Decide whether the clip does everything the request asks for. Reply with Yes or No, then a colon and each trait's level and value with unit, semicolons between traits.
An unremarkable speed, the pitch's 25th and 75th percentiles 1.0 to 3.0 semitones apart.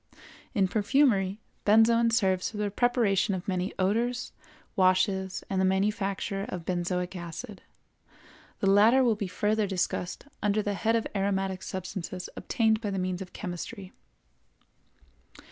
No: slow, 130 wpm; average, 2.7 semitones